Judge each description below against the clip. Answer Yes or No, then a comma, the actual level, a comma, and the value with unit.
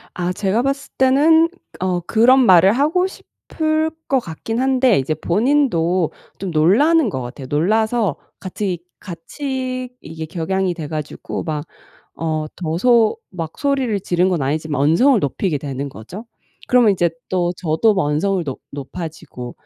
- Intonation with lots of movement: Yes, wide, 7.9 semitones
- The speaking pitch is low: No, medium, 185 Hz